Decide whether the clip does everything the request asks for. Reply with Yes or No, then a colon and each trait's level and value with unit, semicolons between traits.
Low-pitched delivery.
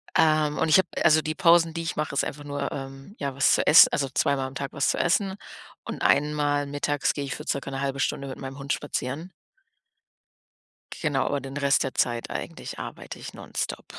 No: medium, 145 Hz